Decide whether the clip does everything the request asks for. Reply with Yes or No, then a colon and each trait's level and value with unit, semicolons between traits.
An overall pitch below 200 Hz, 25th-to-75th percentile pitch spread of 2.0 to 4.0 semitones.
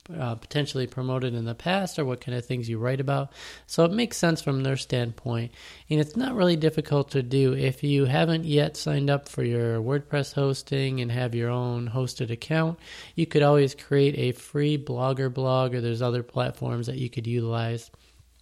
Yes: low, 135 Hz; average, 3.2 semitones